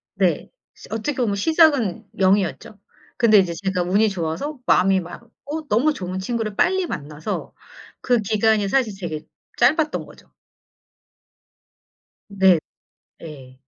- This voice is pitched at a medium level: No, high, 205 Hz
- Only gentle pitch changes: No, average, 5.2 semitones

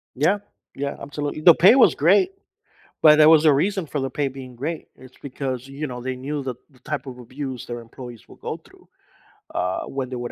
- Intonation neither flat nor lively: Yes, average, 3.0 semitones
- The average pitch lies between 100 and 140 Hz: Yes, low, 135 Hz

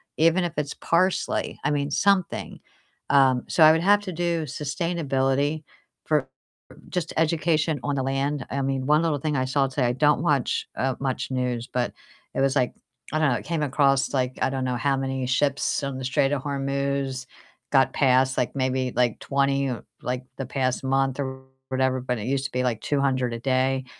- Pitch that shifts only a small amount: Yes, narrow, 2.2 semitones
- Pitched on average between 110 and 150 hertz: Yes, low, 135 Hz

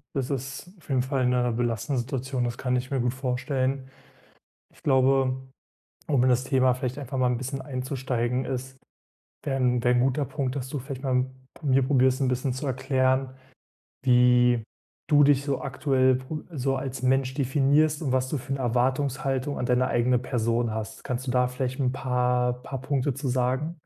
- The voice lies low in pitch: Yes, low, 130 Hz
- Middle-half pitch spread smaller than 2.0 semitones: Yes, narrow, 1.4 semitones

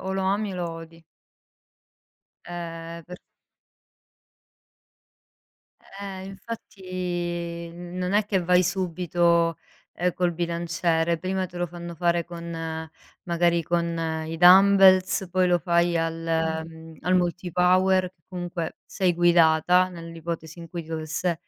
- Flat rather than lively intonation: Yes, narrow, 1.7 semitones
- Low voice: No, medium, 175 Hz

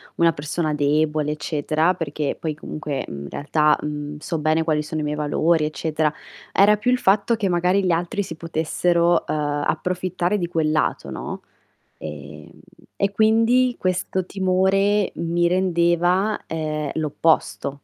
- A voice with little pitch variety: No, average, 3.4 semitones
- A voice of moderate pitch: Yes, medium, 165 Hz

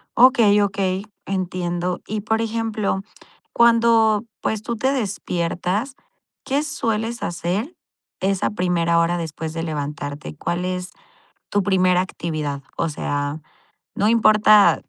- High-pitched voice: Yes, high, 195 Hz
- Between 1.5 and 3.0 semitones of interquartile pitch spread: No, average, 4.4 semitones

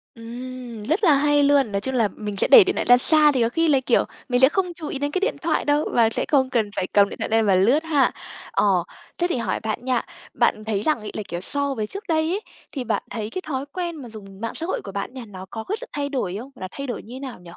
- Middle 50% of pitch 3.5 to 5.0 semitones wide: No, wide, 5.6 semitones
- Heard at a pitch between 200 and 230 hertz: No, very high, 255 Hz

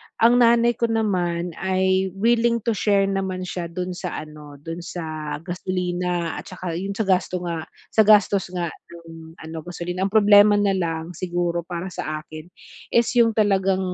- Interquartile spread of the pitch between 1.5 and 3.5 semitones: Yes, average, 3.1 semitones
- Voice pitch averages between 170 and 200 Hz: Yes, medium, 185 Hz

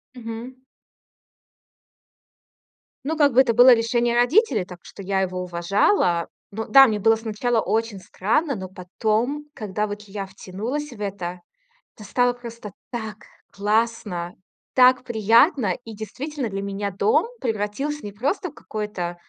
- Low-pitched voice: No, high, 220 Hz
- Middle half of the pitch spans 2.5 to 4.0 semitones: Yes, average, 3.7 semitones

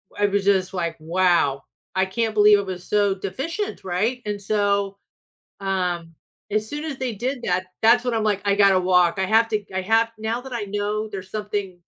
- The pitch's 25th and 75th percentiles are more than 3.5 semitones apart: No, average, 2.8 semitones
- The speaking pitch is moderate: No, high, 200 Hz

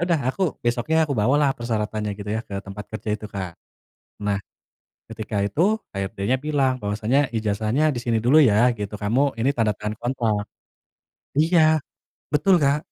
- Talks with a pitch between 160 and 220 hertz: No, low, 115 Hz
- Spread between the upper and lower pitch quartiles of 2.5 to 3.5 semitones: No, average, 5.0 semitones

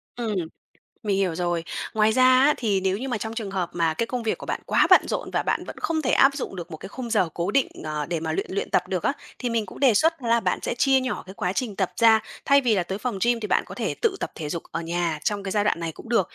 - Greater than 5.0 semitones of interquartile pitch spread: Yes, wide, 5.5 semitones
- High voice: Yes, high, 210 Hz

